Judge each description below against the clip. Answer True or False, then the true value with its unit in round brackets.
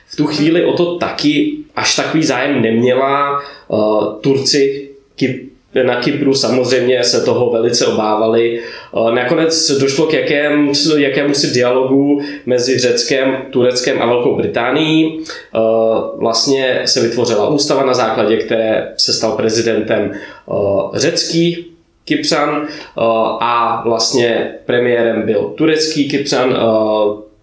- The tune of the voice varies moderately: True (4.4 semitones)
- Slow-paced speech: True (105 wpm)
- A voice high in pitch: False (130 Hz)